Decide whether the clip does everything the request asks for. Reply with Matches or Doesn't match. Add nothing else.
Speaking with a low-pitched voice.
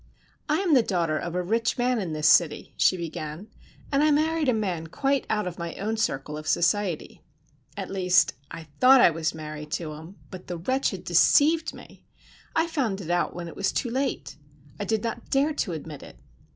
Doesn't match